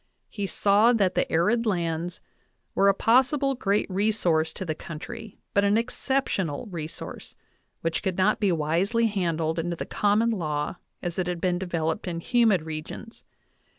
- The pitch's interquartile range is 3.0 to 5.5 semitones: Yes, average, 4.5 semitones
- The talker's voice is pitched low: No, medium, 185 Hz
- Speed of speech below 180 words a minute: Yes, average, 170 wpm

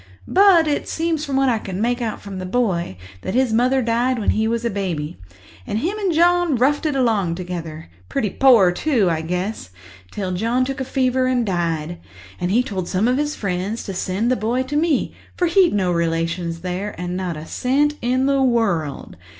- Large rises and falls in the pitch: Yes, wide, 6.6 semitones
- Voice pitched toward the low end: No, high, 220 Hz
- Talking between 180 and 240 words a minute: Yes, average, 200 wpm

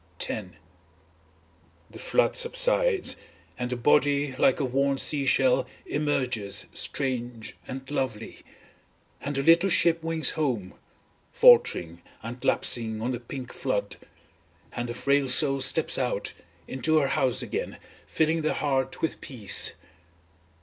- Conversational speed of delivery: No, slow, 130 wpm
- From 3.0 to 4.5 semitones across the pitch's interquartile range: Yes, average, 3.9 semitones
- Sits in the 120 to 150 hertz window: Yes, low, 135 Hz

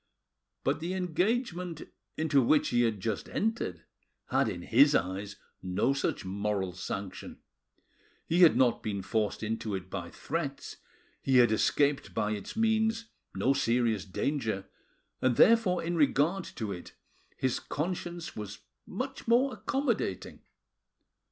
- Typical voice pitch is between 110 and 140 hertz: Yes, low, 135 Hz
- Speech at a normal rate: No, slow, 130 wpm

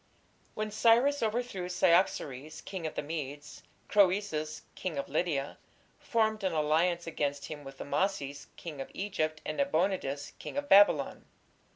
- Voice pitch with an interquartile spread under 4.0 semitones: No, wide, 5.5 semitones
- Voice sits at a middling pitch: Yes, medium, 170 Hz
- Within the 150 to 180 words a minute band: No, average, 140 wpm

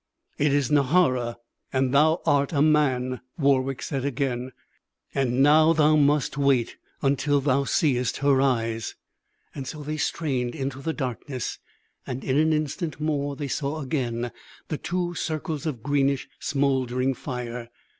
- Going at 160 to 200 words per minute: No, average, 140 wpm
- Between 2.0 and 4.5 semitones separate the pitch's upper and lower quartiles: Yes, average, 2.8 semitones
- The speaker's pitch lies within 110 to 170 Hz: Yes, medium, 140 Hz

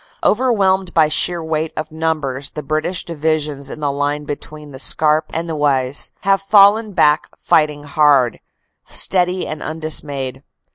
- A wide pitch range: No, average, 2.8 semitones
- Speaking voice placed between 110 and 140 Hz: No, medium, 155 Hz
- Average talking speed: Yes, average, 145 wpm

